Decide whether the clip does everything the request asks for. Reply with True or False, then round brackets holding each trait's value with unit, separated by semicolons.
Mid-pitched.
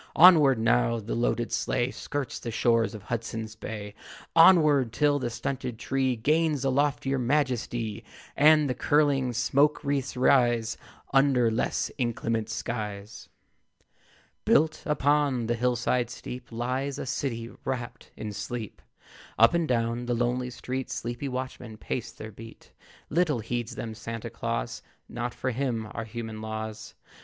False (120 Hz)